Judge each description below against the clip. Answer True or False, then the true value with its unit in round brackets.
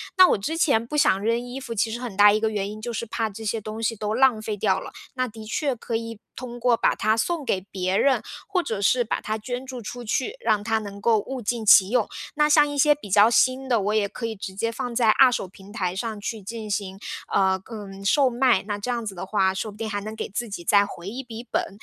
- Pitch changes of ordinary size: True (3.3 semitones)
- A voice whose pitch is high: True (220 Hz)